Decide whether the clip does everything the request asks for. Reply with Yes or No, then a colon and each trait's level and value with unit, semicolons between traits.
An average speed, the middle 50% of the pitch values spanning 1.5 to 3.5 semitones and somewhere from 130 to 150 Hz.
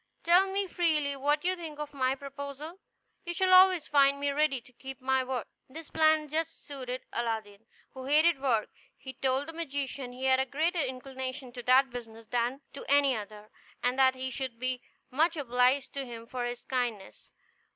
No: average, 185 wpm; average, 3.1 semitones; very high, 270 Hz